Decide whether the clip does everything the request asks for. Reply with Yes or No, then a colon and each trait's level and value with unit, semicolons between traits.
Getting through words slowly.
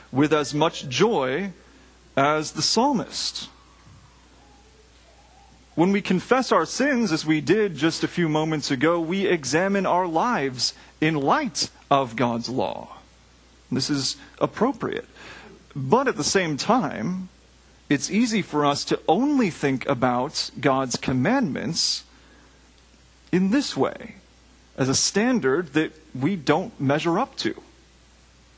Yes: slow, 125 wpm